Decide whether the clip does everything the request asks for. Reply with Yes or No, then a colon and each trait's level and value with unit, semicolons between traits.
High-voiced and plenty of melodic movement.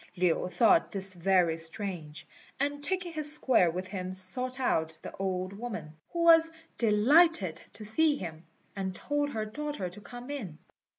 Yes: high, 210 Hz; wide, 7.9 semitones